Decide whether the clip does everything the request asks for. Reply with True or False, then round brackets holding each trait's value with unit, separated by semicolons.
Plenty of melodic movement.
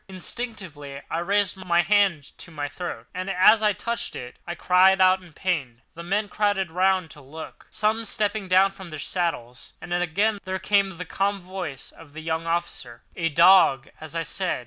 False (3.4 semitones)